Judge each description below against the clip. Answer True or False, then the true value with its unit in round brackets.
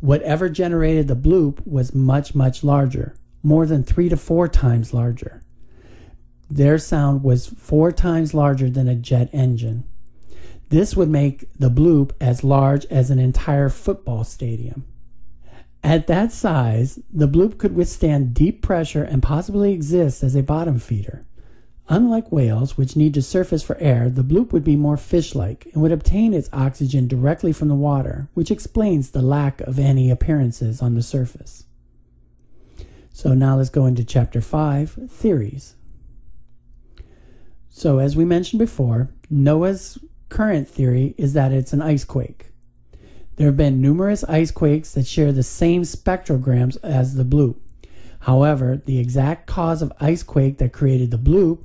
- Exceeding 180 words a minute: False (155 wpm)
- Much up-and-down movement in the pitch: False (4.0 semitones)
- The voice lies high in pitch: False (140 Hz)